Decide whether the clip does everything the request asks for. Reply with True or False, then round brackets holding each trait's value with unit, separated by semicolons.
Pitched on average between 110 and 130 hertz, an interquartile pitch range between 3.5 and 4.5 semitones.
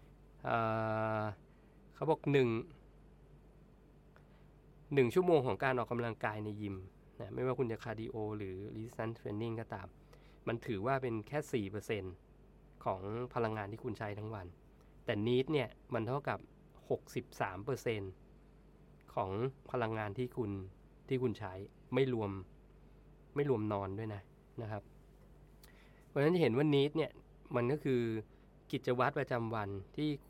True (115 Hz; 4.1 semitones)